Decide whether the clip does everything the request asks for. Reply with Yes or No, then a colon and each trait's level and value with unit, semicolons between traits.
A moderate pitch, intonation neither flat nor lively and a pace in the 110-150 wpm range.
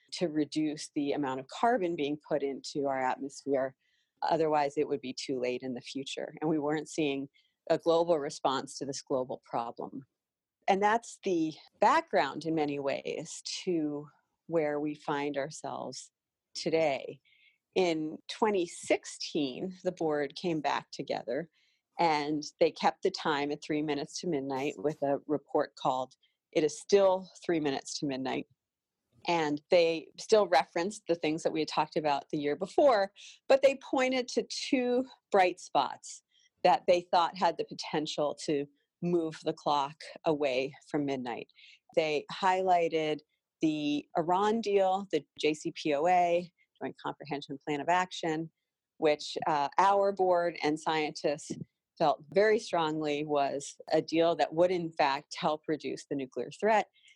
Yes: medium, 155 Hz; average, 3.7 semitones; average, 145 wpm